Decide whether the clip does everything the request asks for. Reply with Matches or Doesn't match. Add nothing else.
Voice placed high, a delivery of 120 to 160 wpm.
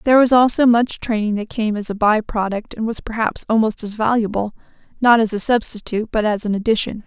Doesn't match